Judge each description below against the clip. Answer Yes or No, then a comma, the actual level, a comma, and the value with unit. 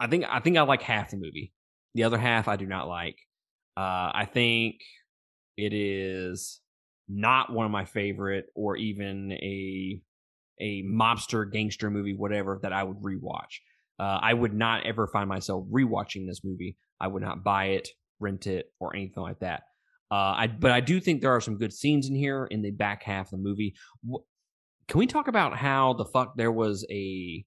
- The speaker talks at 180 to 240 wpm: Yes, average, 195 wpm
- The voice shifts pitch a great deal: No, average, 3.0 semitones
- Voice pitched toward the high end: No, low, 105 Hz